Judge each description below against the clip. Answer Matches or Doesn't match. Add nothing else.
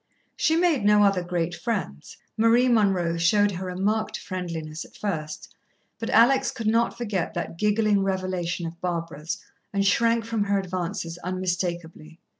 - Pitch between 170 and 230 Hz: Matches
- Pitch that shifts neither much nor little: Matches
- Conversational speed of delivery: Matches